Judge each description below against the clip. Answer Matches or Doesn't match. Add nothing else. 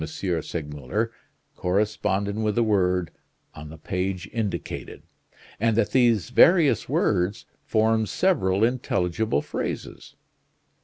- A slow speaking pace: Matches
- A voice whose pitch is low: Matches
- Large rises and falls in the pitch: Doesn't match